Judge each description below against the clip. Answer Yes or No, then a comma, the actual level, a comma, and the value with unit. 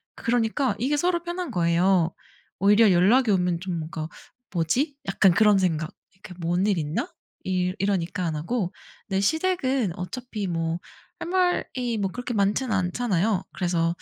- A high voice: Yes, high, 195 Hz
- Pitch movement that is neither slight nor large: No, wide, 5.9 semitones